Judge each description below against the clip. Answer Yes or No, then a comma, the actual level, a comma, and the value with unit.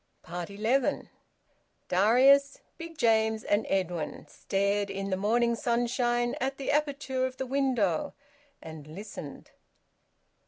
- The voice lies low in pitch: No, high, 230 Hz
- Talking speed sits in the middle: No, slow, 110 wpm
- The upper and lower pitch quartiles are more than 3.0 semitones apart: Yes, average, 4.9 semitones